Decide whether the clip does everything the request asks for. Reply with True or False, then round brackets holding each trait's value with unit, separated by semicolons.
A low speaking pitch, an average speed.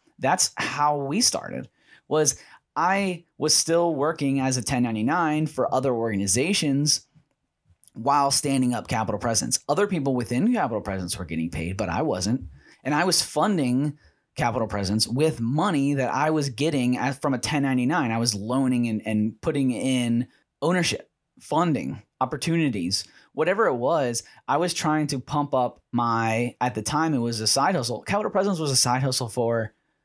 True (130 Hz; 160 wpm)